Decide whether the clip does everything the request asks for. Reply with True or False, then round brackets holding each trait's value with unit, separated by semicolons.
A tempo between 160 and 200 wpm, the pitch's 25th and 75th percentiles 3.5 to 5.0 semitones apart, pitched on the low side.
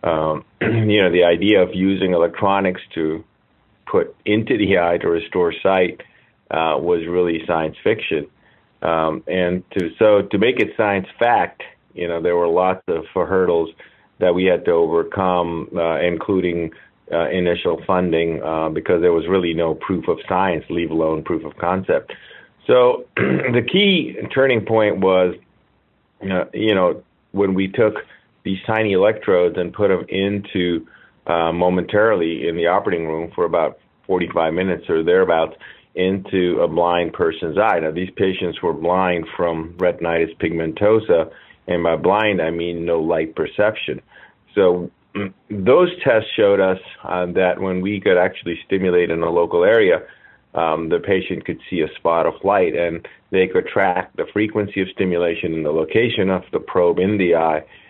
True (165 wpm; 3.8 semitones; 90 Hz)